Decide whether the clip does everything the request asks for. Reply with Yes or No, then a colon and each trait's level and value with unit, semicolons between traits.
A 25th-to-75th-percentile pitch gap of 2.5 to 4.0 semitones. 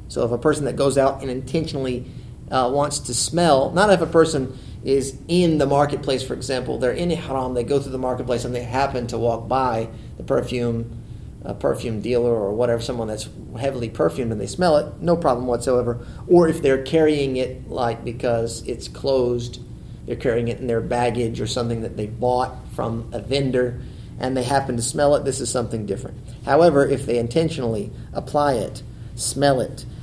Yes: average, 2.8 semitones